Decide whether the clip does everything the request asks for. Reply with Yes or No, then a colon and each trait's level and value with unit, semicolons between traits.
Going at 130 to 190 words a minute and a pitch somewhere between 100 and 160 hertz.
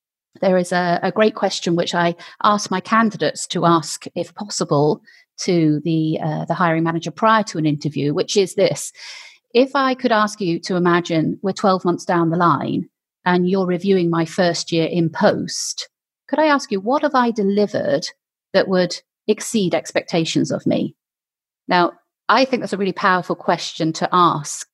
No: average, 175 wpm; medium, 180 Hz